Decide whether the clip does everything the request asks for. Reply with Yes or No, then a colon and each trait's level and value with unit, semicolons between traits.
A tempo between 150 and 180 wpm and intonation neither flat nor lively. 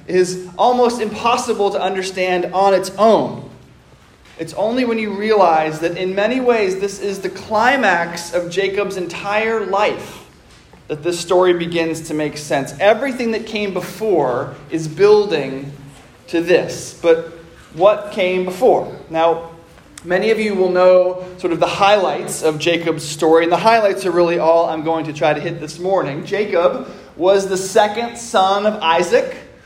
Yes: average, 160 wpm; average, 3.9 semitones